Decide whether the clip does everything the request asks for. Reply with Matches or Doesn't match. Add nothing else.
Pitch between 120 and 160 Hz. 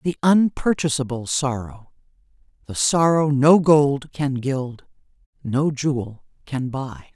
Matches